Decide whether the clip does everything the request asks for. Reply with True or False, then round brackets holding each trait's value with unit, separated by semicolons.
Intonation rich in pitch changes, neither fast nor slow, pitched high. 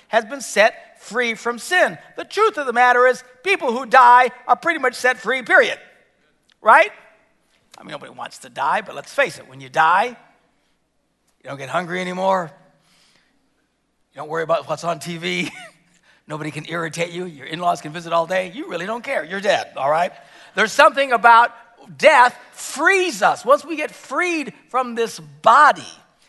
True (7.5 semitones; 180 wpm; 235 Hz)